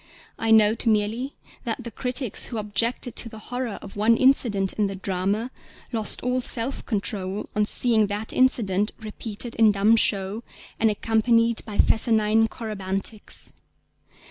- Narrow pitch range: Yes, narrow, 2.2 semitones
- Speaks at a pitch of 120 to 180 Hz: No, high, 220 Hz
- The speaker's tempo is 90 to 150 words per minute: Yes, average, 145 wpm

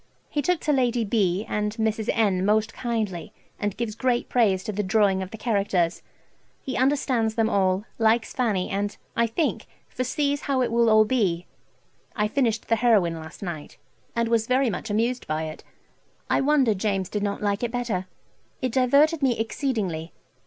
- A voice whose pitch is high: Yes, high, 220 Hz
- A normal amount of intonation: Yes, average, 3.7 semitones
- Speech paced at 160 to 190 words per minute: Yes, average, 175 wpm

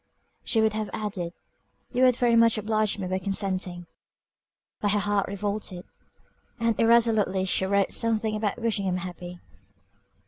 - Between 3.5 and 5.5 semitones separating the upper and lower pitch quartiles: No, average, 2.8 semitones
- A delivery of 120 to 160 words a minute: Yes, average, 145 wpm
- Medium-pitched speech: No, high, 205 Hz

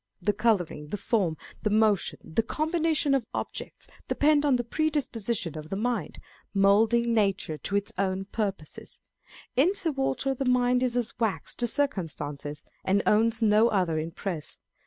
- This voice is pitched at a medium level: No, high, 220 Hz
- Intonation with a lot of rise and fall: No, average, 4.5 semitones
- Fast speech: No, average, 160 wpm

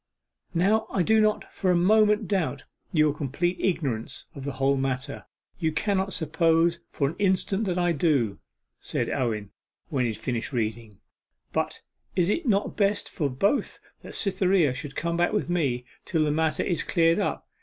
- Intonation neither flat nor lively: No, wide, 5.8 semitones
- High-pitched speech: No, medium, 165 Hz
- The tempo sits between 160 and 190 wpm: Yes, average, 175 wpm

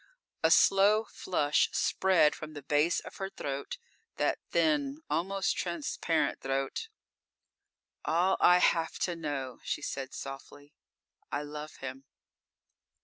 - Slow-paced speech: Yes, slow, 120 wpm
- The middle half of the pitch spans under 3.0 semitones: No, average, 4.8 semitones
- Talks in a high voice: No, medium, 155 Hz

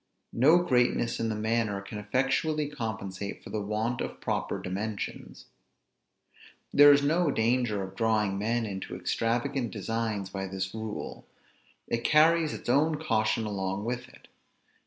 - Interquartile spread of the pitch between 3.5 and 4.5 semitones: Yes, average, 3.8 semitones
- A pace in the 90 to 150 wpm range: Yes, average, 140 wpm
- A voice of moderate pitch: No, low, 115 Hz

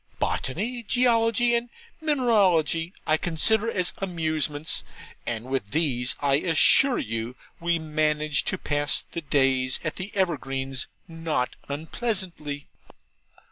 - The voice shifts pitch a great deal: Yes, wide, 5.8 semitones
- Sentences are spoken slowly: Yes, slow, 110 wpm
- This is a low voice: No, medium, 160 Hz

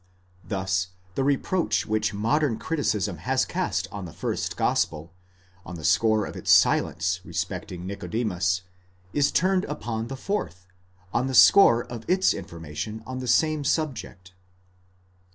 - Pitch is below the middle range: Yes, low, 110 Hz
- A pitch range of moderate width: No, wide, 6.9 semitones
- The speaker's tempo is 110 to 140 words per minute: Yes, slow, 135 wpm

